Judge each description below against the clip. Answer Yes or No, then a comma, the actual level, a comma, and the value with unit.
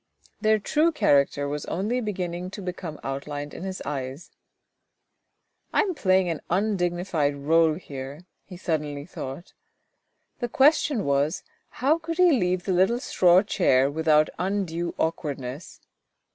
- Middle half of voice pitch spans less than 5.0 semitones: No, wide, 5.6 semitones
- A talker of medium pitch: Yes, medium, 175 Hz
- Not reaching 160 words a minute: Yes, slow, 135 wpm